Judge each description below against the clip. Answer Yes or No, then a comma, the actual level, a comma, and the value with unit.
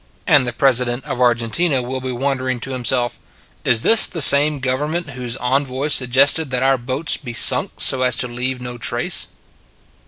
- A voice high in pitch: No, low, 130 Hz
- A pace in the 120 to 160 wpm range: No, average, 180 wpm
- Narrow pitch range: Yes, narrow, 2.1 semitones